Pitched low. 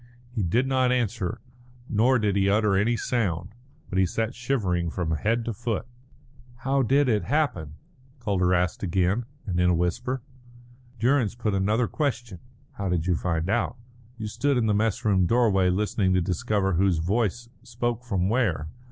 Yes: low, 105 Hz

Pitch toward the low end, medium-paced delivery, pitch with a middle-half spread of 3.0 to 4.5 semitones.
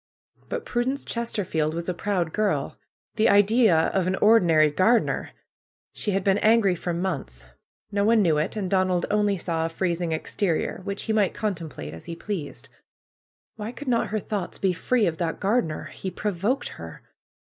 No: high, 190 Hz; average, 170 wpm; average, 4.1 semitones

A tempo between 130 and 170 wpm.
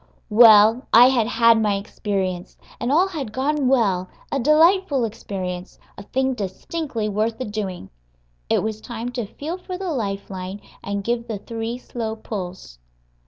Yes: average, 160 wpm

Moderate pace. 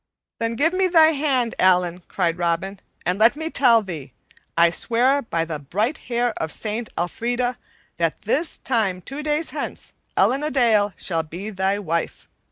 Yes: average, 170 wpm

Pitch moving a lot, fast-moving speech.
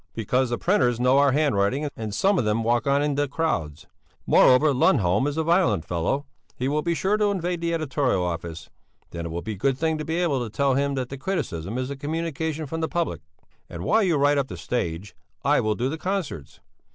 Yes: wide, 6.7 semitones; fast, 225 wpm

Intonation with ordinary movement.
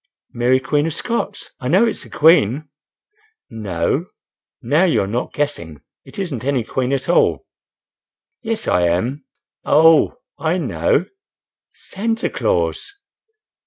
No: wide, 6.7 semitones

